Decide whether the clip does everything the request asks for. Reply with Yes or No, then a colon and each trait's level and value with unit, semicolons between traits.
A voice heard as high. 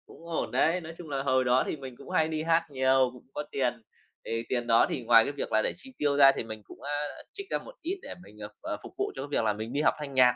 No: low, 135 Hz